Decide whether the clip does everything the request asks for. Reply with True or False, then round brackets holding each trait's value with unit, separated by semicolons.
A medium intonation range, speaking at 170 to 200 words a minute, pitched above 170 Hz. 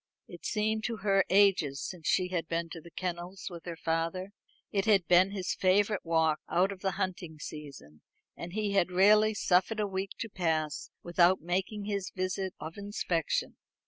True (3.0 semitones; 175 wpm; 185 Hz)